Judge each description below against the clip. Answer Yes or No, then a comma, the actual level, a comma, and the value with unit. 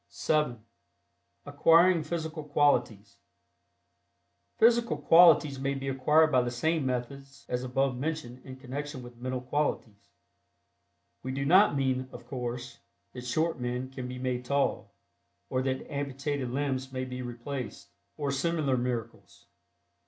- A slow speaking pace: Yes, slow, 130 wpm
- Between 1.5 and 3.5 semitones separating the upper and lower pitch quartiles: Yes, average, 2.7 semitones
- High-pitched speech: No, low, 135 Hz